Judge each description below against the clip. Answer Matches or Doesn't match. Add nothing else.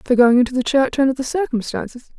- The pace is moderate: Doesn't match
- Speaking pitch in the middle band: Doesn't match